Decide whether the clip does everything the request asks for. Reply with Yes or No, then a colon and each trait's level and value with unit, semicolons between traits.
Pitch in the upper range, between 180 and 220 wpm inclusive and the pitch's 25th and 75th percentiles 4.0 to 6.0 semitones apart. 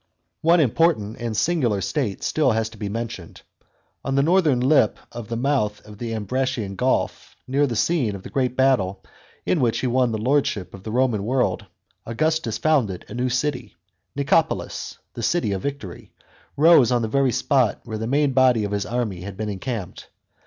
No: low, 120 Hz; average, 185 wpm; average, 4.4 semitones